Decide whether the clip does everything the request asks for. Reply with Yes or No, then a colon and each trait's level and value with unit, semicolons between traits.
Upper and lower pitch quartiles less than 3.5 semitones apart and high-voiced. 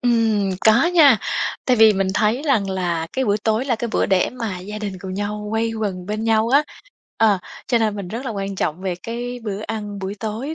Yes: average, 2.8 semitones; high, 215 Hz